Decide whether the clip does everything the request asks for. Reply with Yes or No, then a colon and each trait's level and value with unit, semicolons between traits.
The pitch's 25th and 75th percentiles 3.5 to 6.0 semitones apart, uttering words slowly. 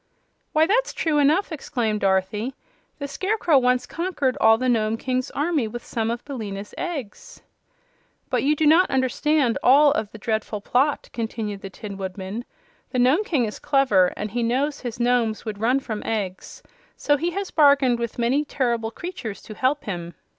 No: average, 5.0 semitones; average, 175 wpm